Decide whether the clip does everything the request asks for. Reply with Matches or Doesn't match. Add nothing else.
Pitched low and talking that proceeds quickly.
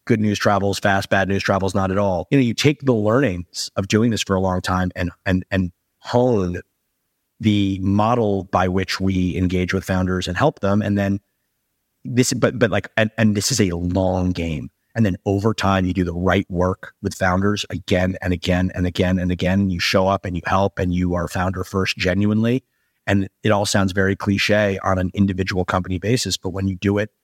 Matches